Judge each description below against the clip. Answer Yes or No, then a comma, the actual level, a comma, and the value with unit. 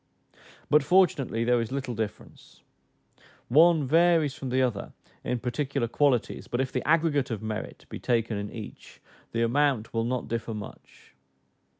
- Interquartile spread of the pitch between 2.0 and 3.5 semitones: No, average, 4.1 semitones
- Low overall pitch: Yes, low, 125 Hz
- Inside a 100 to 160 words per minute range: Yes, average, 155 wpm